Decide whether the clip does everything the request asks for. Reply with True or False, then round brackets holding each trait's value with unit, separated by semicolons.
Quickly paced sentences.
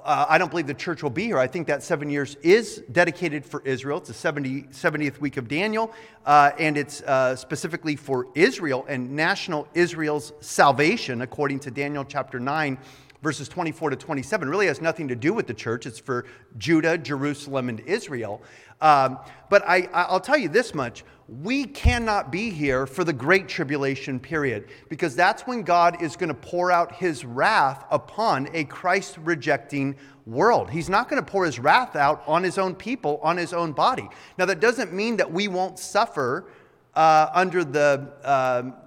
False (185 wpm)